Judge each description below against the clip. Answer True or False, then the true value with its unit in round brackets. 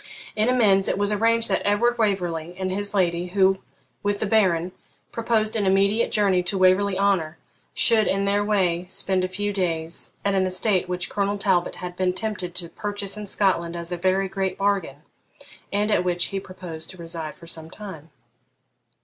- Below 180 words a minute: False (185 wpm)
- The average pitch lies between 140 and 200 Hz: True (190 Hz)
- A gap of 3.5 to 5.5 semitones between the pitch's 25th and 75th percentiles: False (2.4 semitones)